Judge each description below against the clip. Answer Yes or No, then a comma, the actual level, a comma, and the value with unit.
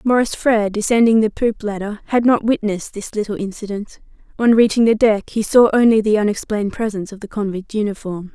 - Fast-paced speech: No, average, 185 wpm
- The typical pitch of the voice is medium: No, high, 215 Hz